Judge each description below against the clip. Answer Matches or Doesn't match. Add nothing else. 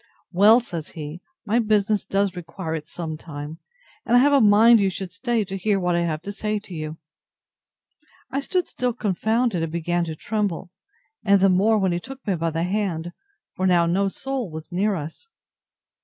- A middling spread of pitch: Matches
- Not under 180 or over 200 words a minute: Matches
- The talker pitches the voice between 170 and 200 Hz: Matches